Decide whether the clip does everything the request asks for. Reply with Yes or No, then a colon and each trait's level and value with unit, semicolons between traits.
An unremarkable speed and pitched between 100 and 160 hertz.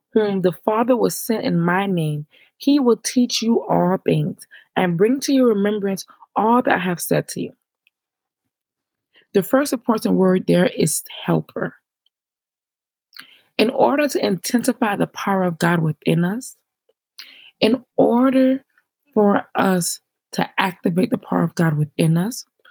No: average, 145 wpm; high, 220 Hz